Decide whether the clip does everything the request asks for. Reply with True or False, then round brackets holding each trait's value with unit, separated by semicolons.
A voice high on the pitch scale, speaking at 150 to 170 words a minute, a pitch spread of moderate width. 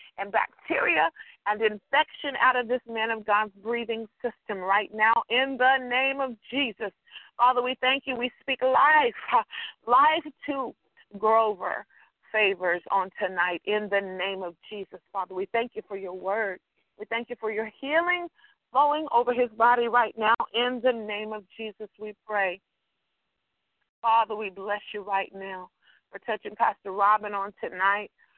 True (220 Hz; 160 wpm; 3.9 semitones)